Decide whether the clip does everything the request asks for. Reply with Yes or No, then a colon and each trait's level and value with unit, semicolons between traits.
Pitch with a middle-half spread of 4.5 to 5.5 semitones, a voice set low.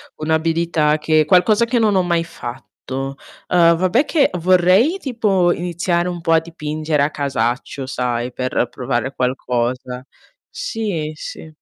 No: average, 5.2 semitones; medium, 160 Hz